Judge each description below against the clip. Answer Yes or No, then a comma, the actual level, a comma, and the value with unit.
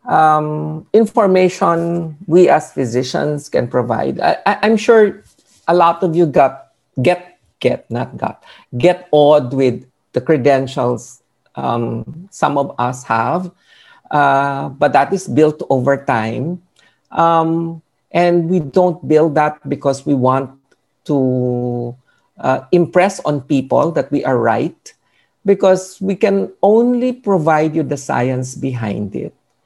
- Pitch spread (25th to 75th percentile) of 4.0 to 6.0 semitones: Yes, average, 5.2 semitones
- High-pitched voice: No, medium, 150 Hz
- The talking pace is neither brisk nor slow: Yes, average, 130 wpm